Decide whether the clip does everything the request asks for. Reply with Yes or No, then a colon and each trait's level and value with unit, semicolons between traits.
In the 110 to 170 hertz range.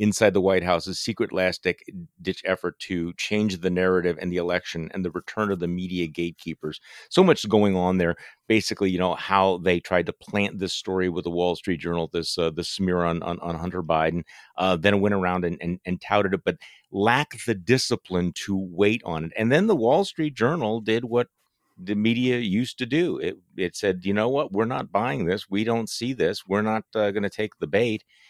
No: very low, 95 Hz